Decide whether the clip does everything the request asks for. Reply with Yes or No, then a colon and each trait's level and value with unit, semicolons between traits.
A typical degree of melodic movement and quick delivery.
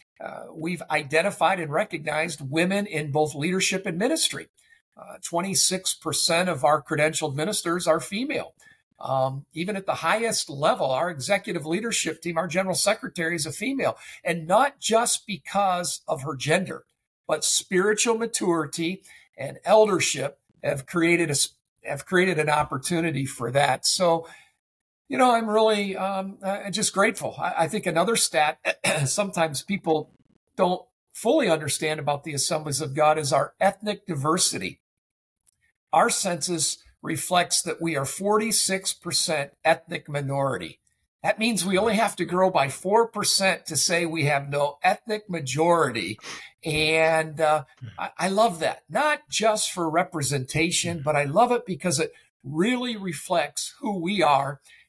No: average, 4.3 semitones; average, 145 wpm